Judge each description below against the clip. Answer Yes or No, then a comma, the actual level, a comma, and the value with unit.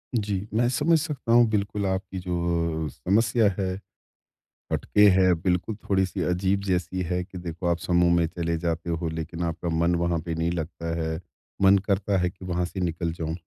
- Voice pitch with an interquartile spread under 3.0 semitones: Yes, narrow, 2.6 semitones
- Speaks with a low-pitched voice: Yes, very low, 90 Hz